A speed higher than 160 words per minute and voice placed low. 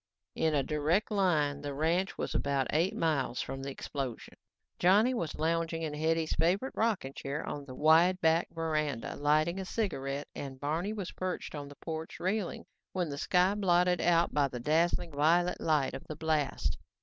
No: average, 185 wpm; medium, 160 Hz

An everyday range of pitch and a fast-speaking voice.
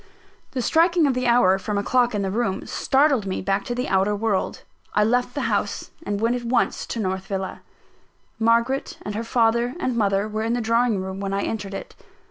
Yes: average, 3.7 semitones; fast, 215 wpm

